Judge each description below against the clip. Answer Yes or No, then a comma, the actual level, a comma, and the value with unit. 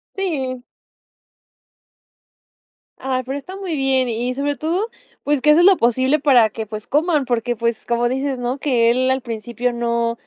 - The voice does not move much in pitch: No, average, 3.4 semitones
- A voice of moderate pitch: No, very high, 255 Hz